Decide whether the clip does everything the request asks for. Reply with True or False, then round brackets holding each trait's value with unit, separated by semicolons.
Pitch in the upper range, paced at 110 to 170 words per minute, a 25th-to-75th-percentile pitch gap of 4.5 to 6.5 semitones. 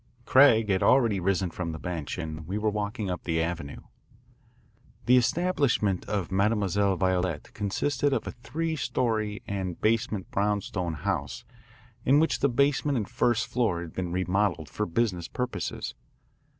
False (105 Hz; 150 wpm; 5.0 semitones)